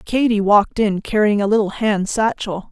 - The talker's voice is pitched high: Yes, high, 210 Hz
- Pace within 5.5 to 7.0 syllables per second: No, 5.0 syllables/s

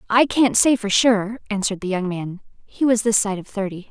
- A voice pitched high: Yes, high, 210 Hz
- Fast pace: Yes, fast, 215 wpm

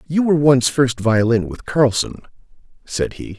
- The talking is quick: No, average, 160 wpm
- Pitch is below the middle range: Yes, low, 130 Hz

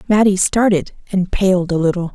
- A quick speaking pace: No, average, 170 wpm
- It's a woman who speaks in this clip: Yes, female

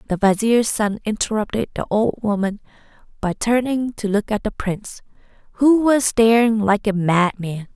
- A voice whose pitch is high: Yes, high, 215 Hz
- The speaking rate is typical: Yes, average, 155 wpm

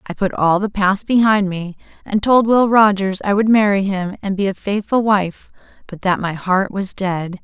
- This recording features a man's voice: No, female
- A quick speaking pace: Yes, fast, 210 wpm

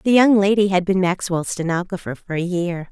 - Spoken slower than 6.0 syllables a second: Yes, 5.4 syllables/s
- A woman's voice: Yes, female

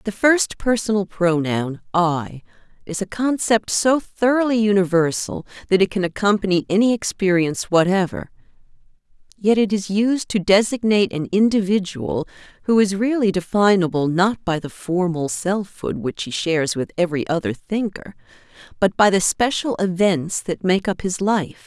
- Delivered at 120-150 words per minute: Yes, average, 145 wpm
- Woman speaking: Yes, female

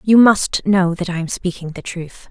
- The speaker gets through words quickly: Yes, fast, 235 wpm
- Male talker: No, female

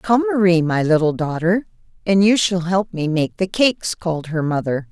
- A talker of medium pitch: Yes, medium, 175 Hz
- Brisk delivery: No, average, 195 wpm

